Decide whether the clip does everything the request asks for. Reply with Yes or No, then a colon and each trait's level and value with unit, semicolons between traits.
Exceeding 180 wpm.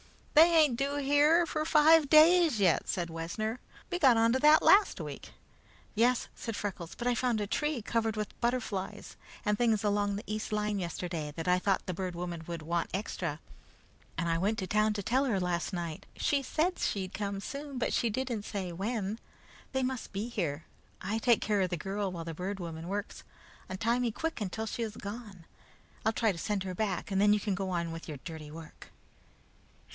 Yes: fast, 205 wpm